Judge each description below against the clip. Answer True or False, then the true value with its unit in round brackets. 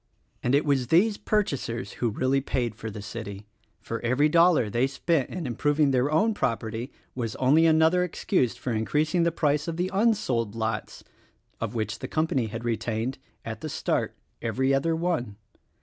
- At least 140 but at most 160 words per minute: False (180 wpm)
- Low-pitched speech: True (130 Hz)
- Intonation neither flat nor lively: False (5.7 semitones)